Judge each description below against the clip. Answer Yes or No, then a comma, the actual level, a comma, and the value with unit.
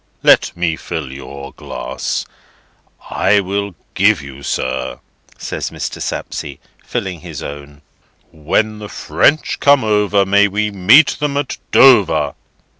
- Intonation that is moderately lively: No, wide, 6.6 semitones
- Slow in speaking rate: Yes, slow, 125 wpm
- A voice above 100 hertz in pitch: No, very low, 95 Hz